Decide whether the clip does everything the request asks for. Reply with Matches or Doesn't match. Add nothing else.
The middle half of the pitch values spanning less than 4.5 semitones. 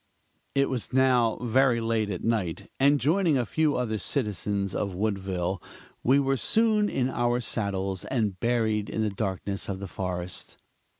Doesn't match